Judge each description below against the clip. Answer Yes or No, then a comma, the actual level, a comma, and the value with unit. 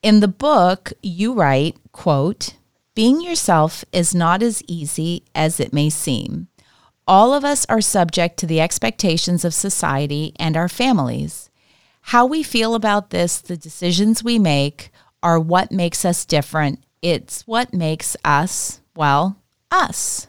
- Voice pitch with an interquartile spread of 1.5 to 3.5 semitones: No, average, 4.9 semitones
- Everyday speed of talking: Yes, average, 145 wpm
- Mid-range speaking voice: Yes, medium, 175 Hz